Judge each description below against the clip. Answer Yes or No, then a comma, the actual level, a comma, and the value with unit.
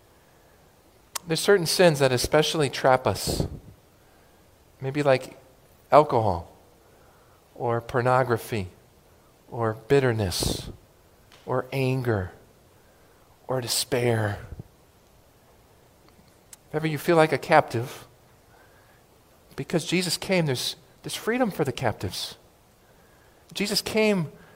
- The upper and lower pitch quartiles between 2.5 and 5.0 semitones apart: No, wide, 5.5 semitones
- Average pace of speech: No, slow, 90 wpm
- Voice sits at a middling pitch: No, low, 130 Hz